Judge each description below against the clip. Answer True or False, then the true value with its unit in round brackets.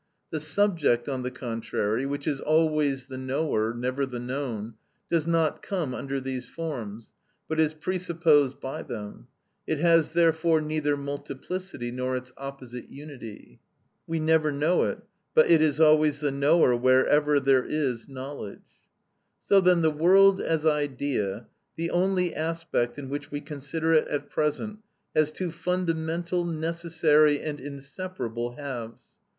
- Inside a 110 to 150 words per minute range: True (145 wpm)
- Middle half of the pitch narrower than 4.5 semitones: True (3.8 semitones)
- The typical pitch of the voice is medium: True (150 Hz)